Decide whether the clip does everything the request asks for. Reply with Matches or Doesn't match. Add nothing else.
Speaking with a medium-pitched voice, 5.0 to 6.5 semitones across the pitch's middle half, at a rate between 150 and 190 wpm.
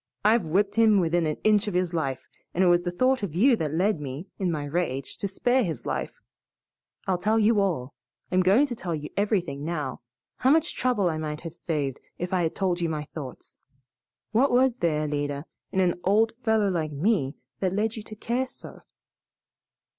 Doesn't match